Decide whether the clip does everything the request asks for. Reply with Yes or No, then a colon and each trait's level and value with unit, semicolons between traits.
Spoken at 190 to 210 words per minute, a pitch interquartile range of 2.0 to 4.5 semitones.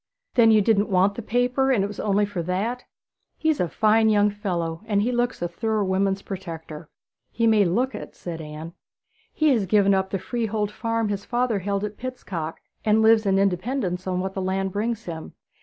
Yes: average, 200 wpm; average, 3.2 semitones